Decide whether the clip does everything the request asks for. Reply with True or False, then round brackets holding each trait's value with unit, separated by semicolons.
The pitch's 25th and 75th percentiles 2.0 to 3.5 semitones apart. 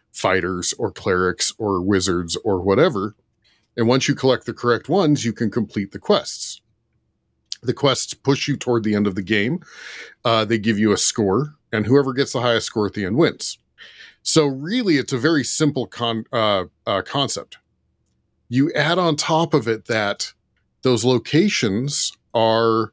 False (4.5 semitones)